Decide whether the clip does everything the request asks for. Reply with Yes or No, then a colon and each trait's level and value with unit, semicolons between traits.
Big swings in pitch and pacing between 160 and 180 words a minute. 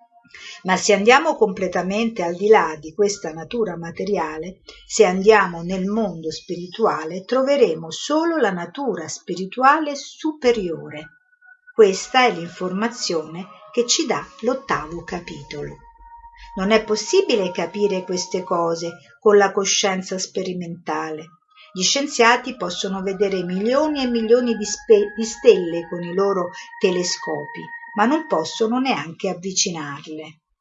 No: wide, 5.7 semitones; average, 120 wpm